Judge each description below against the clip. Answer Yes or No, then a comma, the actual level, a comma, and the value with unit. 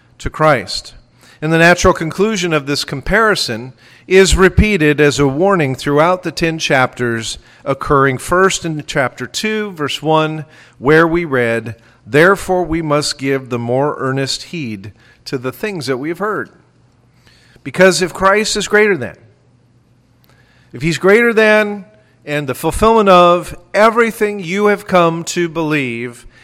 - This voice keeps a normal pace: Yes, average, 145 wpm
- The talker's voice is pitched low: No, medium, 155 Hz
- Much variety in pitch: Yes, wide, 6.6 semitones